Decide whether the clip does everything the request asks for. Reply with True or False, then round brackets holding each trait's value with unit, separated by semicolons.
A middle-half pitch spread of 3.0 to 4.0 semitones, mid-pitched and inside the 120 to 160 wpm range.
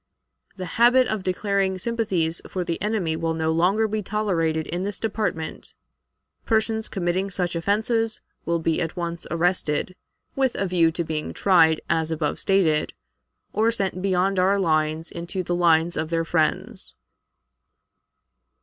True (3.6 semitones; 180 Hz; 145 wpm)